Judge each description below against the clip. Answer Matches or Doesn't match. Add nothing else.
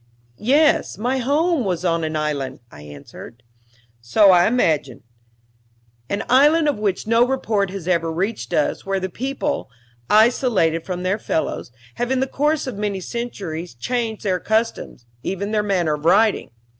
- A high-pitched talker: Matches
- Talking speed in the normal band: Matches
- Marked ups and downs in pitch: Matches